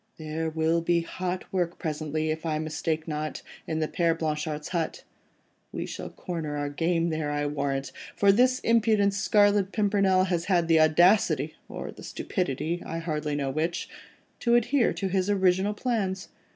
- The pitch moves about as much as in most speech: Yes, average, 3.8 semitones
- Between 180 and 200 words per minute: No, average, 155 wpm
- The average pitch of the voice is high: No, medium, 165 Hz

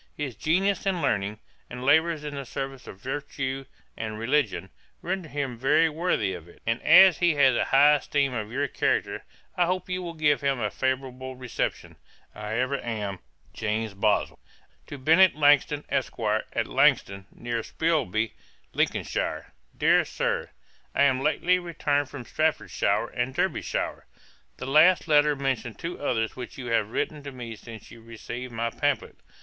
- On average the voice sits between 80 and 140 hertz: Yes, low, 135 Hz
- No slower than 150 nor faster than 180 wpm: Yes, average, 165 wpm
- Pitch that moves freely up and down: No, average, 4.6 semitones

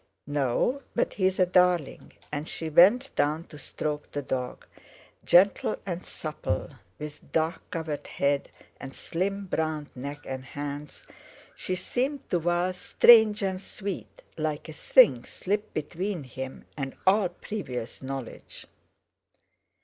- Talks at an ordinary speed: No, slow, 130 wpm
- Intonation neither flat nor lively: Yes, average, 4.7 semitones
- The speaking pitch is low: No, medium, 160 Hz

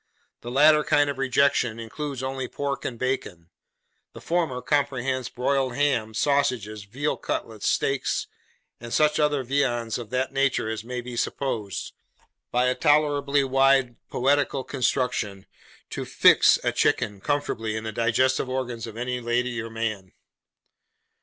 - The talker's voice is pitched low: Yes, low, 125 Hz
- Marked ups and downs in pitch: No, average, 3.3 semitones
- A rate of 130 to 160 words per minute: Yes, average, 140 wpm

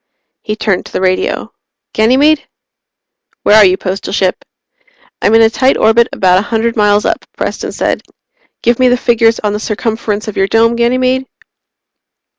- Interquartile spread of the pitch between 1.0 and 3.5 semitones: Yes, narrow, 2.5 semitones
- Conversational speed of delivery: Yes, average, 165 wpm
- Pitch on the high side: Yes, high, 225 Hz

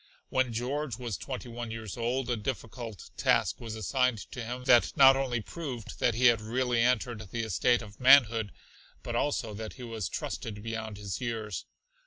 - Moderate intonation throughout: No, narrow, 2.3 semitones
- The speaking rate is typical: Yes, average, 180 wpm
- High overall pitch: No, low, 120 Hz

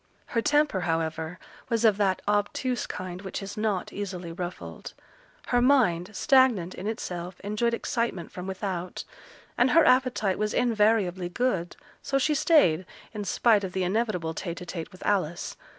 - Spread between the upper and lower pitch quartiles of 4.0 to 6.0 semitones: Yes, average, 4.7 semitones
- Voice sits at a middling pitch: No, high, 200 Hz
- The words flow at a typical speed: Yes, average, 155 wpm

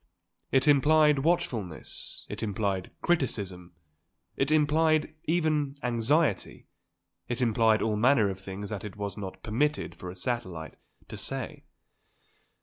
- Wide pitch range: Yes, wide, 6.9 semitones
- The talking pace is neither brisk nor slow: No, slow, 125 wpm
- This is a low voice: Yes, low, 115 Hz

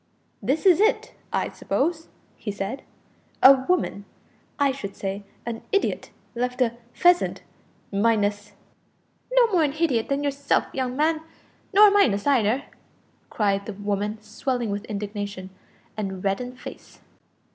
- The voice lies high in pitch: Yes, high, 240 Hz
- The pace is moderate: Yes, average, 145 wpm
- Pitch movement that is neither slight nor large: No, wide, 5.9 semitones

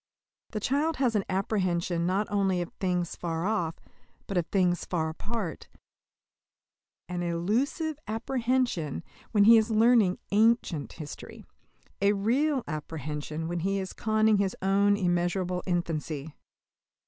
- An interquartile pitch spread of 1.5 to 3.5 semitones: No, average, 4.2 semitones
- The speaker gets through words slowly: Yes, slow, 125 wpm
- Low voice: No, high, 190 Hz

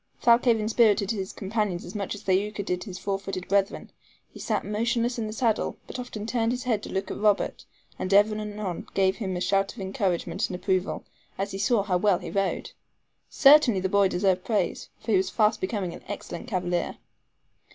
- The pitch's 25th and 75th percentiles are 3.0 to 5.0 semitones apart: No, narrow, 2.5 semitones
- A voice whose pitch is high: Yes, high, 200 Hz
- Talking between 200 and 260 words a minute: Yes, fast, 205 wpm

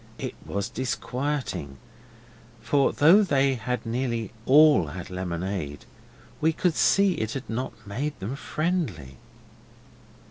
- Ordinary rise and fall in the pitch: No, wide, 7.2 semitones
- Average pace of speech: No, slow, 115 wpm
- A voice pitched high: No, low, 125 Hz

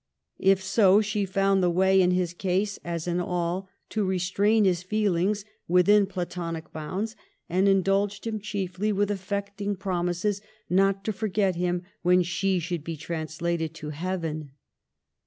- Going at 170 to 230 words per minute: No, average, 145 wpm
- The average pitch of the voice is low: No, medium, 185 Hz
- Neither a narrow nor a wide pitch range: No, narrow, 2.3 semitones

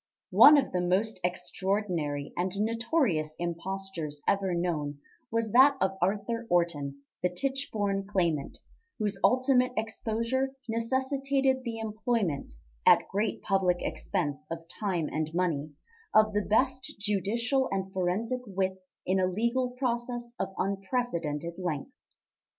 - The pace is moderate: No, slow, 120 wpm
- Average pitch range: Yes, average, 5.0 semitones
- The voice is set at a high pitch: Yes, high, 195 Hz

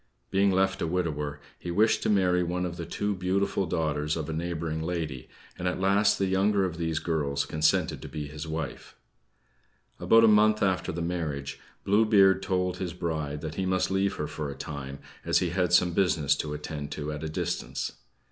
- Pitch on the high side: No, very low, 85 Hz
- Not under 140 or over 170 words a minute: No, average, 200 wpm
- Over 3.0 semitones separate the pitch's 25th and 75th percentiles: Yes, average, 3.6 semitones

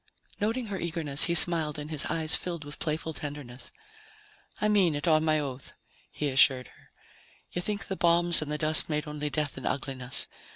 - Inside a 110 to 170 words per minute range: No, average, 190 wpm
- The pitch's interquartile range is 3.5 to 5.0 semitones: No, average, 2.8 semitones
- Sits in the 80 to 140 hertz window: No, medium, 155 Hz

